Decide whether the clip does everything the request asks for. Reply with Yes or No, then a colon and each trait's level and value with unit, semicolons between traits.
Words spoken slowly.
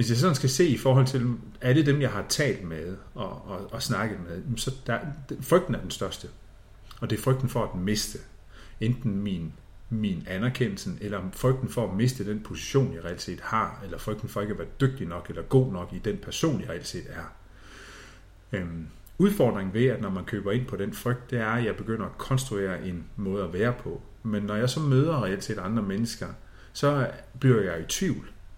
No: average, 215 wpm